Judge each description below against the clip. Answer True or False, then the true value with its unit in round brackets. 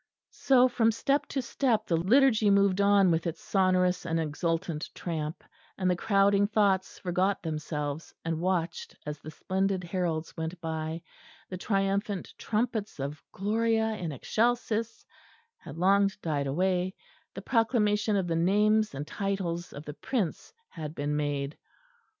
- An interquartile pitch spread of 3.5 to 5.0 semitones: True (4.3 semitones)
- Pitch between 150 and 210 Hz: True (185 Hz)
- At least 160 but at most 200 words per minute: False (145 wpm)